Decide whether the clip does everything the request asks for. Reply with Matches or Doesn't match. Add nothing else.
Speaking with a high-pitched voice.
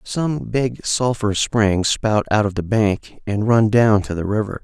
Doesn't match